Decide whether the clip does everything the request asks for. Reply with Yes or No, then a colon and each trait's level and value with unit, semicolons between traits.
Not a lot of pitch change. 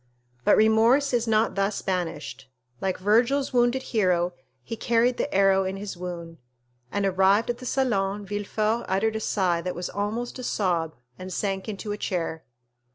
No: average, 3.8 semitones